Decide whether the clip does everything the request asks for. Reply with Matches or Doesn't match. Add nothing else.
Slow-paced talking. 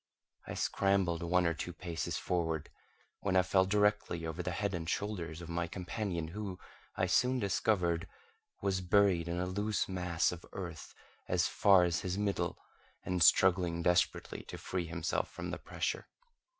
Doesn't match